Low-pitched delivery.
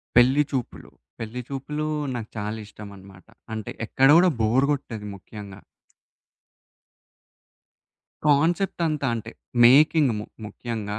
Yes: low, 120 Hz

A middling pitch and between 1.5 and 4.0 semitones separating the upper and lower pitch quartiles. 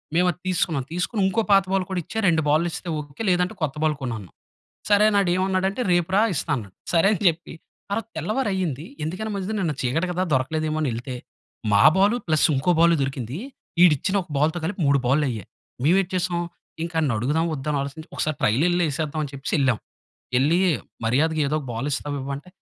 No: medium, 160 Hz; average, 4.7 semitones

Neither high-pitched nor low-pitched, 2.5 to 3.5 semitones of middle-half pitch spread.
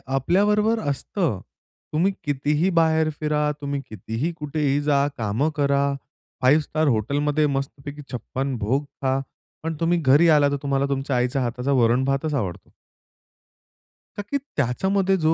Yes: medium, 145 Hz; average, 2.8 semitones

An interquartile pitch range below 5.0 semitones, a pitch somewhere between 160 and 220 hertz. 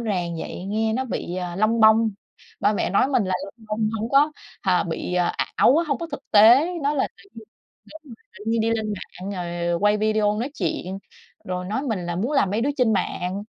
Yes: average, 3.8 semitones; high, 215 Hz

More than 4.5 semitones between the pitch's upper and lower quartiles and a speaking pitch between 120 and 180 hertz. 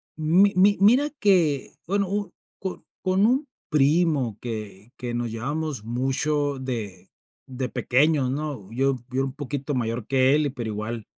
Yes: average, 5.1 semitones; low, 135 Hz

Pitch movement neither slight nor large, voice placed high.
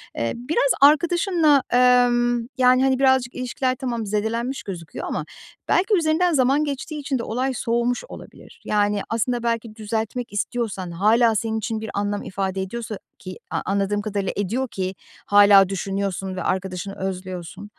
Yes: average, 4.3 semitones; high, 230 Hz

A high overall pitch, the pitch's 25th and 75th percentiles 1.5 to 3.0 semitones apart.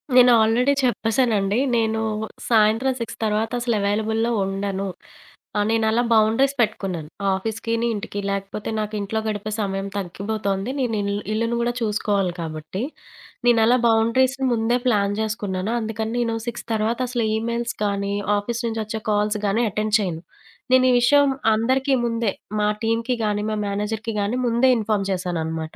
Yes: high, 220 Hz; narrow, 2.4 semitones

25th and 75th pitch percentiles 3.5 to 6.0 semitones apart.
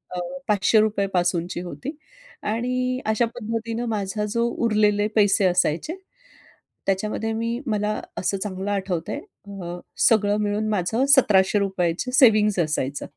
No: average, 3.1 semitones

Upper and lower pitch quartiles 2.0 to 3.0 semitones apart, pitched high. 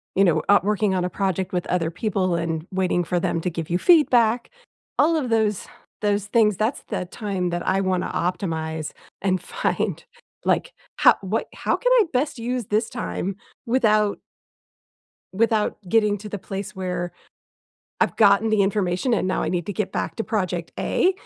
No: average, 3.5 semitones; high, 195 Hz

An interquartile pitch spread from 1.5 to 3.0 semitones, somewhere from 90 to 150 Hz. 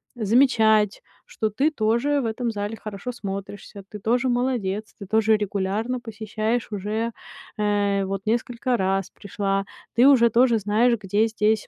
No: average, 2.7 semitones; high, 220 Hz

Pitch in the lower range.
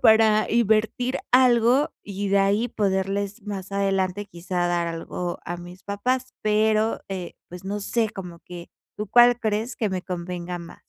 No: high, 200 Hz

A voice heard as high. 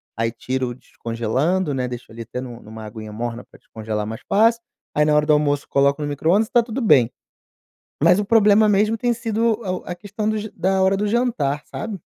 No: medium, 155 Hz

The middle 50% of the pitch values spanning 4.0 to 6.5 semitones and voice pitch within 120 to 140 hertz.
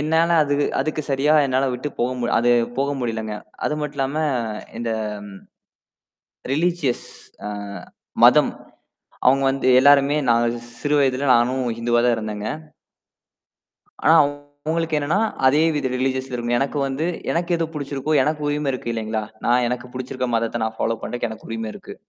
No: average, 3.6 semitones; low, 135 Hz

